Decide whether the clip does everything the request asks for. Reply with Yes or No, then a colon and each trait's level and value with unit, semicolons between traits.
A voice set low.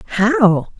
No: high, 225 Hz